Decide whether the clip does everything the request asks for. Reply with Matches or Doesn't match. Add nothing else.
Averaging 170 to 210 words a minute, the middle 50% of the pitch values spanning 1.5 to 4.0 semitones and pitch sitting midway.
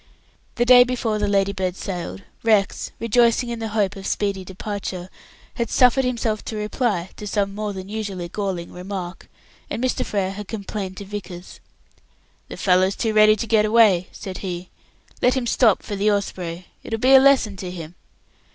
Doesn't match